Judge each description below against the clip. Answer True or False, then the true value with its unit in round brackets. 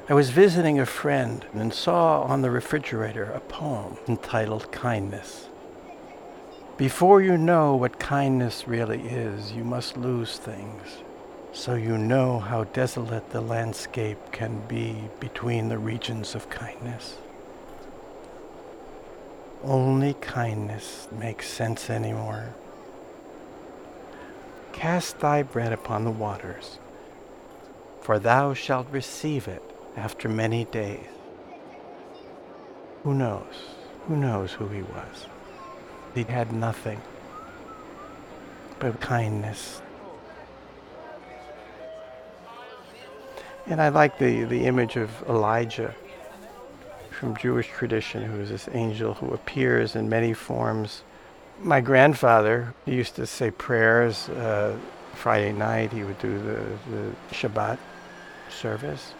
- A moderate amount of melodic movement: True (3.3 semitones)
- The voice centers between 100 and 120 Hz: True (115 Hz)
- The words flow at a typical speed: False (110 wpm)